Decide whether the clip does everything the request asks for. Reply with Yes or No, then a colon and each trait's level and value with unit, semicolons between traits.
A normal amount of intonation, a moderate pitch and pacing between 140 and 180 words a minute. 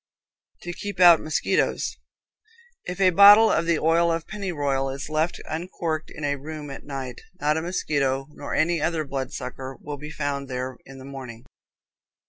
Yes: average, 3.8 semitones; medium, 150 Hz; average, 170 wpm